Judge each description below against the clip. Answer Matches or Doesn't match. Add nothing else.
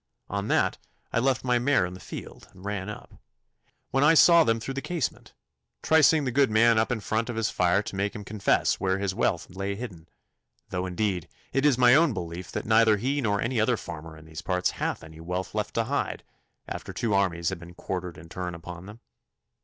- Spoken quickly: Matches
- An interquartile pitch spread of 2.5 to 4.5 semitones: Doesn't match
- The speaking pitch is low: Matches